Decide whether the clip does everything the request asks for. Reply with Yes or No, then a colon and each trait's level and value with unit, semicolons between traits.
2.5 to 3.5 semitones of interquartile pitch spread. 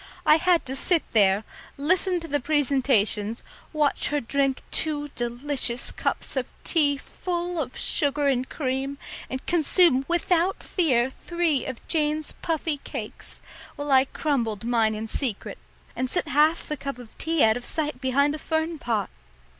No: average, 4.1 semitones